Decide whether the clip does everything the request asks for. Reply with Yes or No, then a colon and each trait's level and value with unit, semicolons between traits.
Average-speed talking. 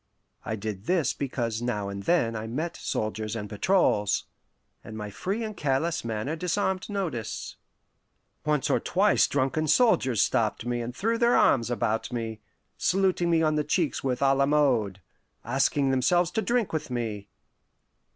Yes: average, 155 wpm